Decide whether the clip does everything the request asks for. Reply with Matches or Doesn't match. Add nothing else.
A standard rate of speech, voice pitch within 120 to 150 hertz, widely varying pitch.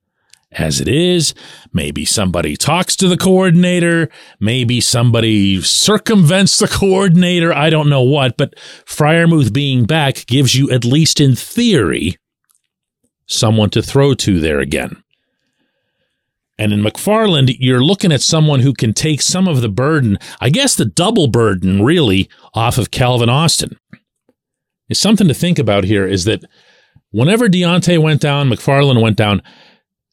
Matches